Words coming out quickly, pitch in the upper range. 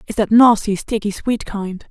No: average, 190 wpm; high, 210 Hz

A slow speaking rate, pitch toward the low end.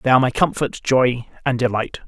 No: average, 200 wpm; low, 125 Hz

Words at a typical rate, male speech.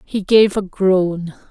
No: average, 160 wpm; female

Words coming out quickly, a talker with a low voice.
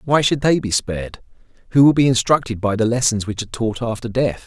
Yes: fast, 230 wpm; low, 120 Hz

